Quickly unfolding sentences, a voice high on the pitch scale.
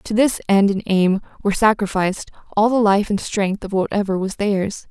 No: average, 195 wpm; high, 200 Hz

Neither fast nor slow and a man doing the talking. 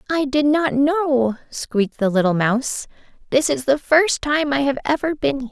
No: average, 195 wpm; female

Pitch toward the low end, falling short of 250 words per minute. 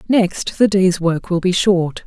No: medium, 185 Hz; fast, 205 wpm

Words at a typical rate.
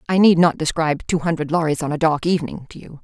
No: fast, 255 wpm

